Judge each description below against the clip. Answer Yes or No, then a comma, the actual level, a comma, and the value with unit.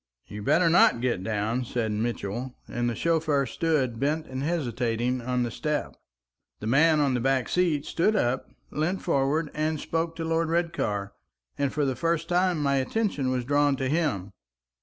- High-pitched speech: No, medium, 140 Hz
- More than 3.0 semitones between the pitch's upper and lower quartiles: Yes, average, 5.1 semitones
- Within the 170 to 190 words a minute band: Yes, average, 175 wpm